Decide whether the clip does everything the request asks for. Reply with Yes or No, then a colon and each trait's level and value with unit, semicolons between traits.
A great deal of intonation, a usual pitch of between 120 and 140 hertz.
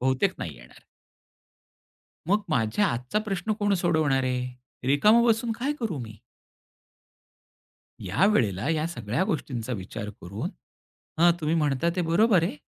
No: wide, 8.7 semitones; medium, 155 Hz